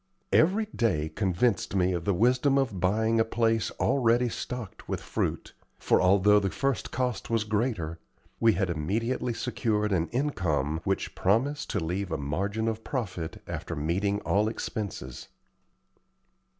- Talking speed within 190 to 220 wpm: No, average, 145 wpm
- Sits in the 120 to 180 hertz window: No, low, 105 Hz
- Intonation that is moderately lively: Yes, average, 4.3 semitones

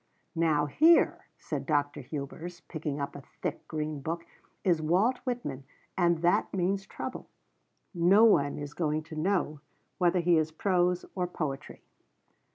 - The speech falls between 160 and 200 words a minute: No, average, 145 wpm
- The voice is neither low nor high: Yes, medium, 165 Hz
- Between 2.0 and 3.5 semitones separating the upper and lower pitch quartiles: Yes, average, 3.2 semitones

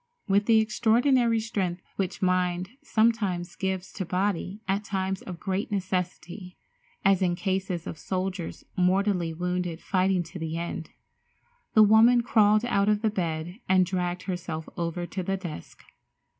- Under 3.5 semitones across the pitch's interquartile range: Yes, narrow, 2.5 semitones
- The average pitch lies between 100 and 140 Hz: No, high, 190 Hz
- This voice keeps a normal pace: Yes, average, 145 wpm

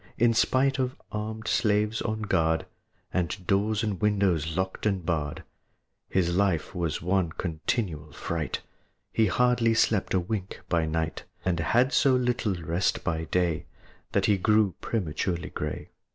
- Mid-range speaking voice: No, very low, 95 Hz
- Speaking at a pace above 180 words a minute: No, average, 145 wpm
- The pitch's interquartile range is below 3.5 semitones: No, average, 4.6 semitones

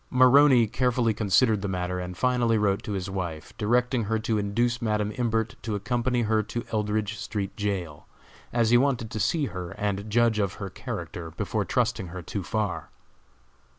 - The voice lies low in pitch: Yes, low, 110 Hz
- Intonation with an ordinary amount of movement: Yes, average, 3.3 semitones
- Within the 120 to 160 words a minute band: No, average, 175 wpm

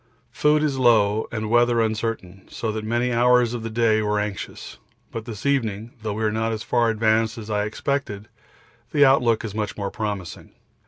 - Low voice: Yes, low, 110 Hz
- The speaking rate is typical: Yes, average, 190 wpm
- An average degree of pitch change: No, narrow, 2.0 semitones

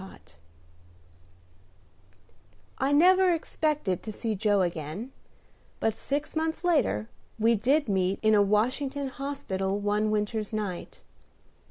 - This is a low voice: No, high, 220 Hz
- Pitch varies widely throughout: Yes, wide, 5.9 semitones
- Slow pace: Yes, slow, 115 wpm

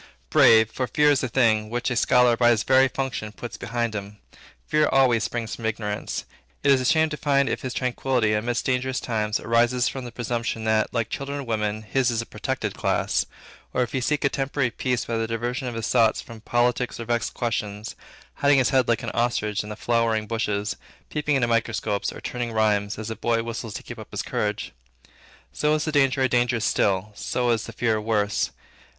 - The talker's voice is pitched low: Yes, low, 120 Hz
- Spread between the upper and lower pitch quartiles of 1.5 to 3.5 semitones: Yes, average, 2.7 semitones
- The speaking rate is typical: No, fast, 210 wpm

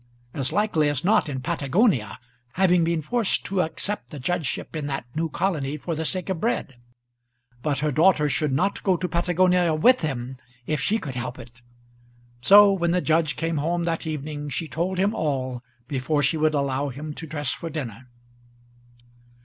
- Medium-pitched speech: Yes, medium, 155 Hz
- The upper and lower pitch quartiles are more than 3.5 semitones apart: Yes, average, 4.1 semitones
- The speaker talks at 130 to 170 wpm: No, average, 180 wpm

